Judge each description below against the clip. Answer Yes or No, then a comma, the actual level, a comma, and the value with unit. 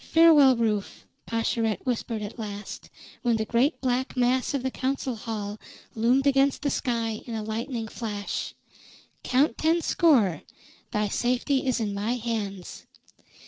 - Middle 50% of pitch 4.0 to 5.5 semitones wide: No, average, 3.3 semitones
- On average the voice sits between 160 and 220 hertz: No, high, 235 Hz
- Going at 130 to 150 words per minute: Yes, average, 145 wpm